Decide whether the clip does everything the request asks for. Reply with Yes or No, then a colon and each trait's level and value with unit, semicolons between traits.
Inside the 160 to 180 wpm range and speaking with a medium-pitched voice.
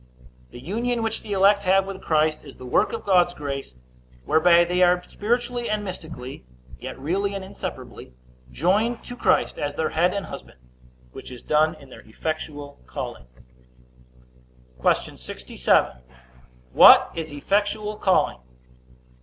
No: average, 140 wpm; medium, 180 Hz